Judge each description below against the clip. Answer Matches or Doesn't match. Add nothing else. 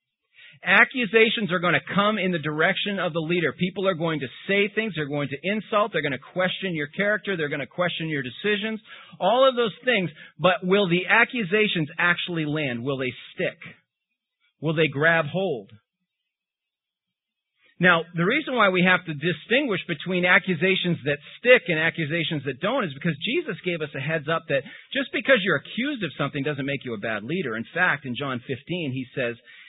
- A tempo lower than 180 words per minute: Doesn't match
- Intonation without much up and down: Doesn't match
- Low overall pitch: Doesn't match